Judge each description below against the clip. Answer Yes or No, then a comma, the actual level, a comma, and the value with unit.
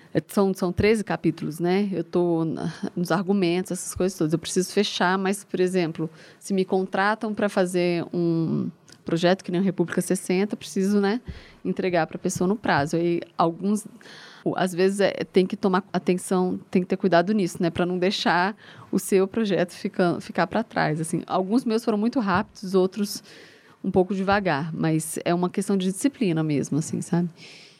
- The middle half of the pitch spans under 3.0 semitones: Yes, narrow, 2.6 semitones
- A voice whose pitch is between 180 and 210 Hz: Yes, medium, 185 Hz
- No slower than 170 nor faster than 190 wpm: Yes, average, 180 wpm